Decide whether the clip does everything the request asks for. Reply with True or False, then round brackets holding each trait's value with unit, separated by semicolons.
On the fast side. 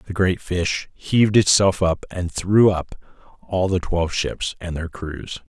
False (175 wpm)